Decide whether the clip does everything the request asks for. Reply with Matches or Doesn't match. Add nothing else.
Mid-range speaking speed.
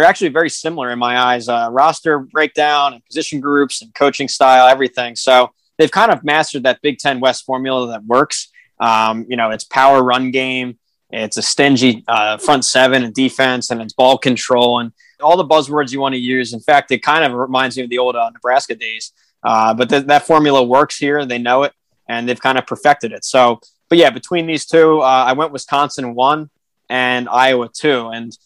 Doesn't match